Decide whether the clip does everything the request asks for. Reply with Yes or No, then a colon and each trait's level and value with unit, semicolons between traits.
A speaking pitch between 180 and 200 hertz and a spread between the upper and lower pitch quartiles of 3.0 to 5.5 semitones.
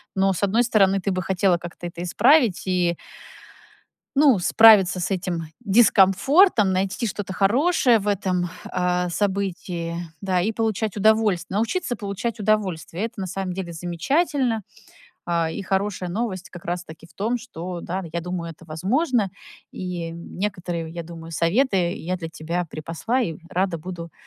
Yes: high, 190 Hz; average, 3.6 semitones